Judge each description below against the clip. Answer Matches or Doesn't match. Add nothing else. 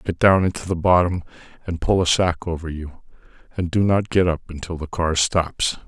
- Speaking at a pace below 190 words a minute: Doesn't match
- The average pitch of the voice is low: Matches